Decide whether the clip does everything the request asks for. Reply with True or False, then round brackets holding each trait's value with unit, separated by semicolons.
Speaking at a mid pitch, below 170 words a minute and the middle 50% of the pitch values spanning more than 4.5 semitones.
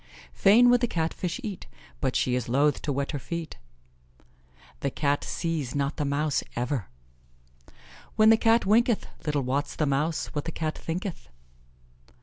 True (150 Hz; 160 wpm; 5.4 semitones)